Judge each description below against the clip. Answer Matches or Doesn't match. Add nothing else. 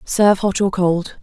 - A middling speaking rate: Matches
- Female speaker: Matches